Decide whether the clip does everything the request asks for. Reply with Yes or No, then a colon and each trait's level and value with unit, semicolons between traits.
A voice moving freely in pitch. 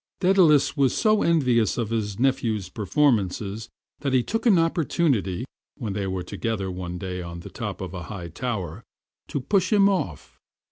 Yes: wide, 7.8 semitones